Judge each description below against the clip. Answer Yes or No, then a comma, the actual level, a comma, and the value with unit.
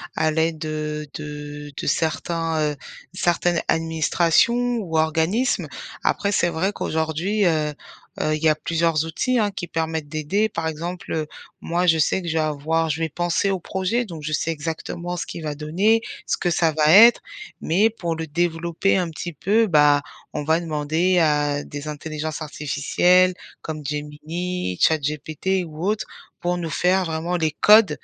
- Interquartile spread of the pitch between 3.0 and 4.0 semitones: No, narrow, 2.6 semitones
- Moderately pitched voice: Yes, medium, 160 Hz